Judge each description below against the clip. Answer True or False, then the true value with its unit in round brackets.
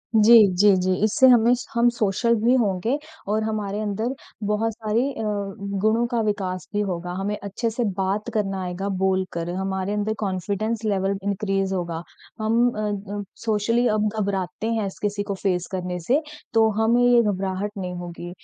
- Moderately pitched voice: False (205 Hz)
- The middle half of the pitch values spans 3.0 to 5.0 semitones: False (2.5 semitones)